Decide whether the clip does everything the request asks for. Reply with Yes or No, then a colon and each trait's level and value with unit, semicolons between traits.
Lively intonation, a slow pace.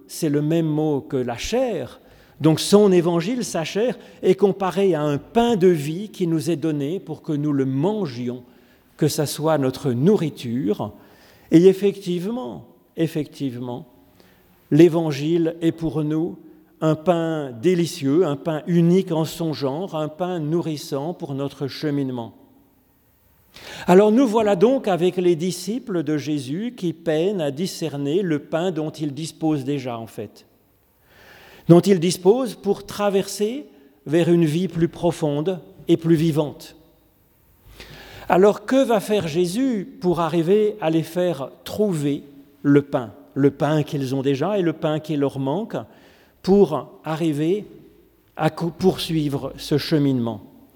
No: average, 4.2 semitones; slow, 140 wpm